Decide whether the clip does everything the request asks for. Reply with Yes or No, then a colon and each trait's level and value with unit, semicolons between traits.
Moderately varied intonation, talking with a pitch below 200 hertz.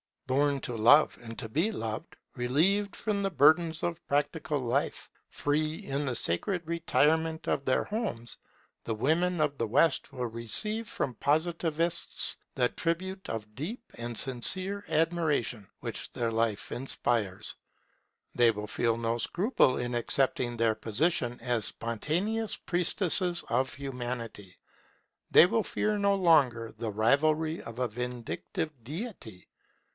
No: wide, 6.4 semitones; medium, 140 Hz